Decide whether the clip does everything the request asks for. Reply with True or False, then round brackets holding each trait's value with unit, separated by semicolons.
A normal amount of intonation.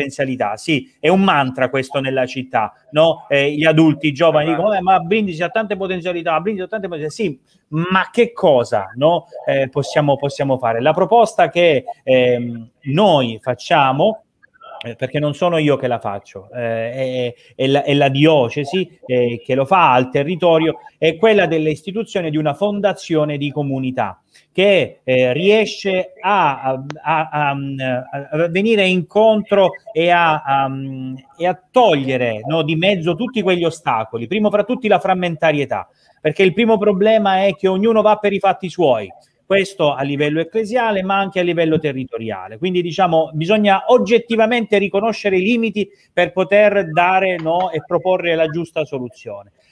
False (6.0 semitones)